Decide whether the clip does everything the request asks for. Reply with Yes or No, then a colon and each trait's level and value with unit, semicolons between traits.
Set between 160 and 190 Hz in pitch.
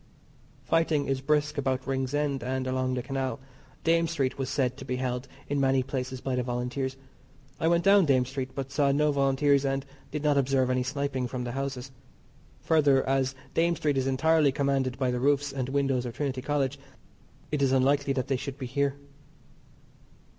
No: low, 135 Hz